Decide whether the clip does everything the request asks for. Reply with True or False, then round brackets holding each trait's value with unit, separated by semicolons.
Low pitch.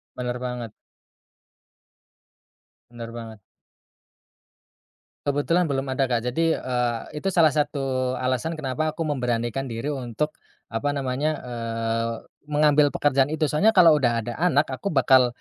True (130 Hz)